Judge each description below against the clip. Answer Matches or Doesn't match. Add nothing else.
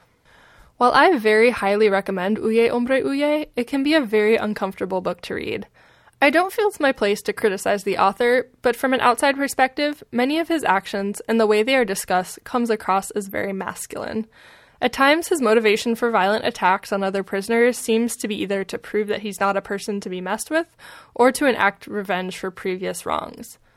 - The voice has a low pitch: Doesn't match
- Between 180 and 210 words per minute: Matches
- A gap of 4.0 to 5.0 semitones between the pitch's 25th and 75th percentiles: Matches